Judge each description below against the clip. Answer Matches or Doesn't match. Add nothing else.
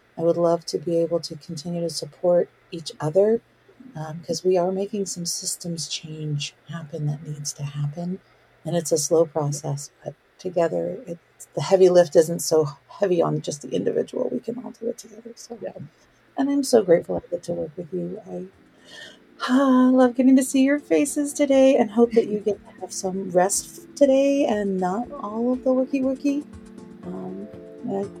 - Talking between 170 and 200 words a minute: Matches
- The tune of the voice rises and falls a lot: Matches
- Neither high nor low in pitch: Matches